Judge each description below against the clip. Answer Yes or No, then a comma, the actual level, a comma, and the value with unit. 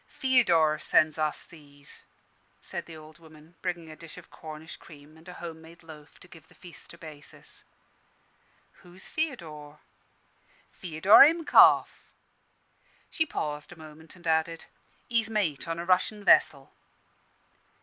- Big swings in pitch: No, narrow, 2.6 semitones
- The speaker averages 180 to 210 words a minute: No, average, 140 wpm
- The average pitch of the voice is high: No, medium, 160 Hz